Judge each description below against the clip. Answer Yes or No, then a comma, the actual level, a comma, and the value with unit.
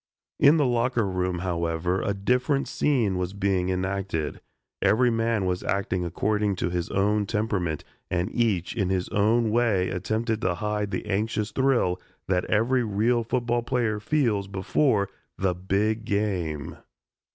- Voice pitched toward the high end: No, low, 105 Hz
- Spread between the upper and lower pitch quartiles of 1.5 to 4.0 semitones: Yes, average, 3.7 semitones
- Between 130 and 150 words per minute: Yes, average, 145 wpm